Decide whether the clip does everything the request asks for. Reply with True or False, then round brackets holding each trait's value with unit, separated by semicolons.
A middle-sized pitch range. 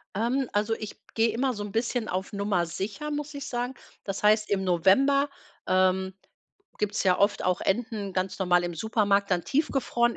True (4.1 semitones)